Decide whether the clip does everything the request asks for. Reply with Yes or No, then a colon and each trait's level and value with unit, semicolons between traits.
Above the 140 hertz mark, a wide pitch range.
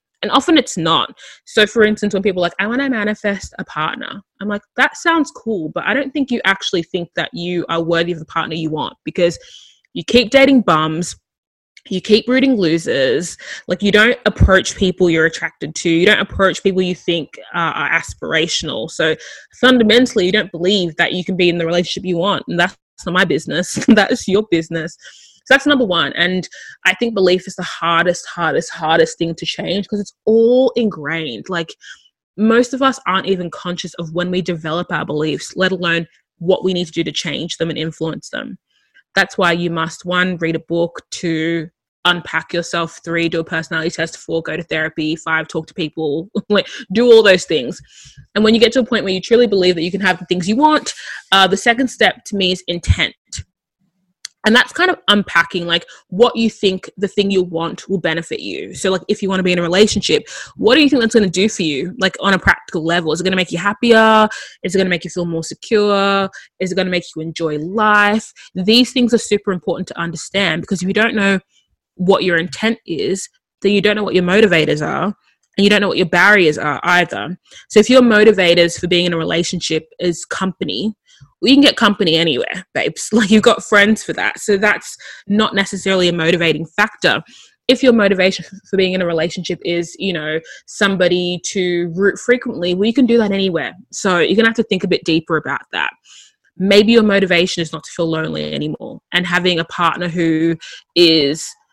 No: medium, 185 Hz; average, 3.7 semitones